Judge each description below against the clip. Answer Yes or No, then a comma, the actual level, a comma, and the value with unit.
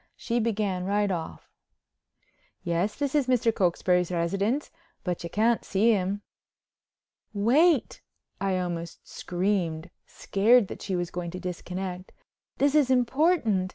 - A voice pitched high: Yes, high, 195 Hz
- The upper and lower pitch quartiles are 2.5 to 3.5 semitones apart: No, average, 4.5 semitones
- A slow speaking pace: Yes, slow, 125 wpm